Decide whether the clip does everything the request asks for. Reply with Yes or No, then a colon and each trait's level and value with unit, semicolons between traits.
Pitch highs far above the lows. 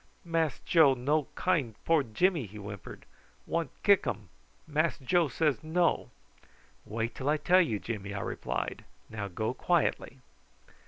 Yes: wide, 7.2 semitones